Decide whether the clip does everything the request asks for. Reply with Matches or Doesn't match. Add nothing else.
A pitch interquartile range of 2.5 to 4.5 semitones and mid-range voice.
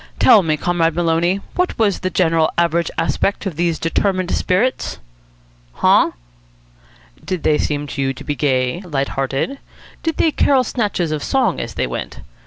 Matches